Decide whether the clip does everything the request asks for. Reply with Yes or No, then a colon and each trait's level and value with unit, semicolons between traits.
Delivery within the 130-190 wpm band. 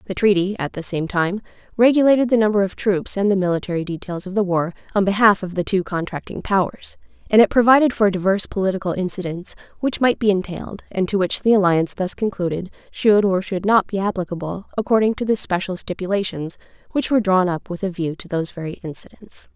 No: average, 200 wpm